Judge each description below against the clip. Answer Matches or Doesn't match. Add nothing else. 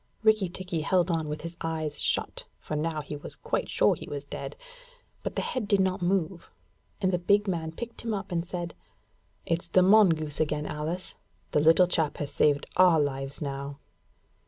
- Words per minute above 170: Matches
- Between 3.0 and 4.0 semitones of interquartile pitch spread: Matches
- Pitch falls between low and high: Matches